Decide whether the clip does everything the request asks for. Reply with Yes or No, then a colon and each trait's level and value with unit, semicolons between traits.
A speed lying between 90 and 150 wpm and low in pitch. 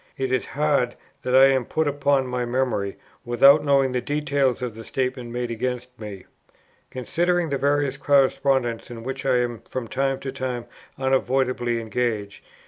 No: average, 160 wpm; low, 130 Hz